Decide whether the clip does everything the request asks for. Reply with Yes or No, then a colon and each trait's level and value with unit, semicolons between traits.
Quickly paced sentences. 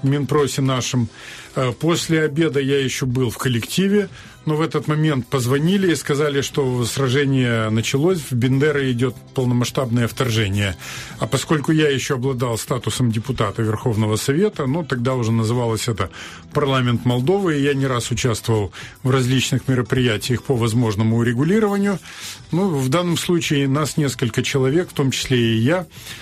No: average, 145 wpm